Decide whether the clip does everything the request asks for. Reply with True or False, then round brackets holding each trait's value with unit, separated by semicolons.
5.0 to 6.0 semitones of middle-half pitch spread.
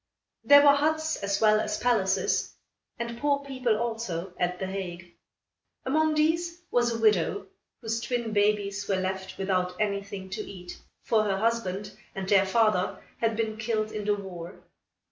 False (3.6 semitones)